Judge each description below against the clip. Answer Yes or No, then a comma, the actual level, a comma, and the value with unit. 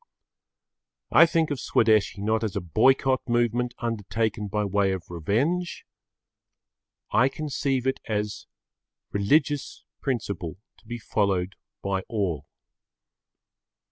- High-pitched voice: No, low, 110 Hz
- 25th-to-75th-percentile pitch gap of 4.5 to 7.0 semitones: Yes, average, 4.8 semitones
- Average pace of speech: No, slow, 110 wpm